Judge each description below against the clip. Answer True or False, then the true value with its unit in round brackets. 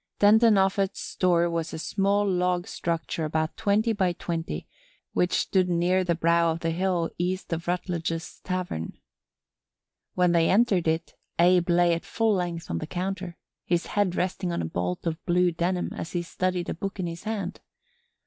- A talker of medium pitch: True (175 Hz)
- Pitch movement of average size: False (1.9 semitones)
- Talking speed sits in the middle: True (175 wpm)